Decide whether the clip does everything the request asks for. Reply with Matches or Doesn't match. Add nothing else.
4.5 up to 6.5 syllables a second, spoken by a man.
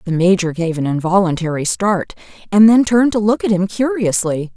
Doesn't match